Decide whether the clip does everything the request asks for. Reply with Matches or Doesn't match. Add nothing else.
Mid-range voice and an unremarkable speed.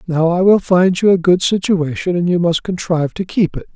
Doesn't match